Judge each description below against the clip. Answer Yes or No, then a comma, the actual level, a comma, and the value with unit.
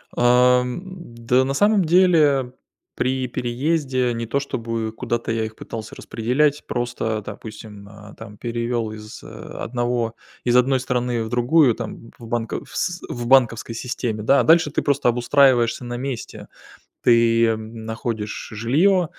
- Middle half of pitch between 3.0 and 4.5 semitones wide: No, narrow, 2.6 semitones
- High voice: No, low, 120 Hz